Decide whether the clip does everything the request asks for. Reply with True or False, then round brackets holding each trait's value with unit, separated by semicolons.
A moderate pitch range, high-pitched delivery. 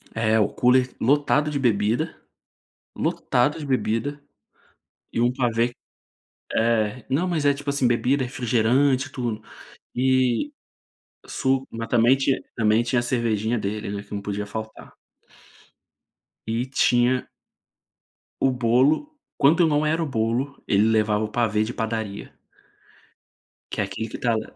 False (3.4 semitones; 120 Hz)